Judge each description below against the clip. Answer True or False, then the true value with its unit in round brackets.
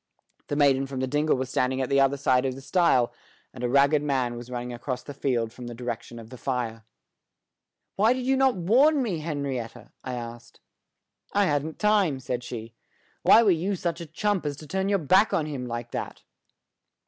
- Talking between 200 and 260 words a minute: True (205 wpm)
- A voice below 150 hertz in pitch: True (140 Hz)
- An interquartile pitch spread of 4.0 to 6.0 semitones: True (5.6 semitones)